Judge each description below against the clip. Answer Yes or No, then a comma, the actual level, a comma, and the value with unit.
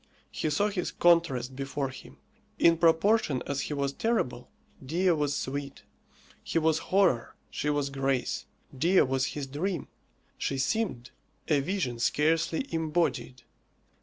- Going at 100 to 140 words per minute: Yes, slow, 135 wpm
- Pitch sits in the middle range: Yes, medium, 150 Hz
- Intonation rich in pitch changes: No, average, 3.9 semitones